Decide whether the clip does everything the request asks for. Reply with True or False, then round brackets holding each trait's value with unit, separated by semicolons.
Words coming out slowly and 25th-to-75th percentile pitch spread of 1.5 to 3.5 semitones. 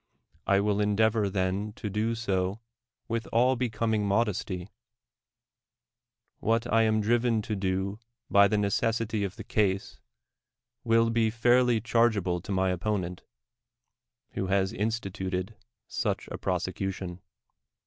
True (125 wpm; 2.9 semitones)